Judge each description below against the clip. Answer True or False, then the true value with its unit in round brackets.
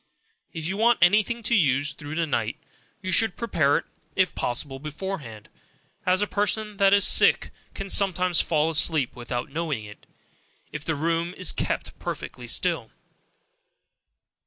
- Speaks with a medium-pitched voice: True (165 Hz)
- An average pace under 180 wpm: True (155 wpm)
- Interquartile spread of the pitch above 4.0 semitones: True (5.3 semitones)